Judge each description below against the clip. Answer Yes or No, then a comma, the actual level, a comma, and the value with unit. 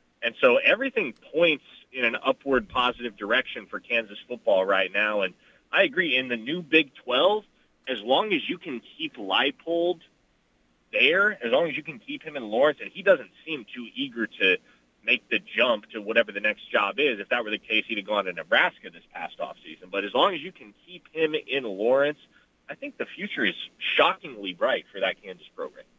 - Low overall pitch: No, medium, 165 Hz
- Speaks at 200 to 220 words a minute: Yes, fast, 205 wpm